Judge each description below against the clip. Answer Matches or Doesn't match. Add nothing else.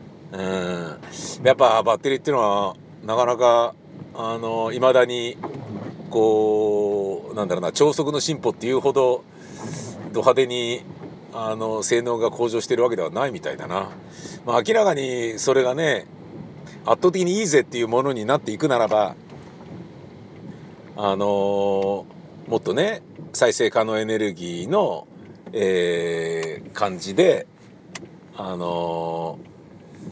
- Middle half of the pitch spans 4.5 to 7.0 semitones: Matches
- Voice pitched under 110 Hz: Doesn't match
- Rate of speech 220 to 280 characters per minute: Matches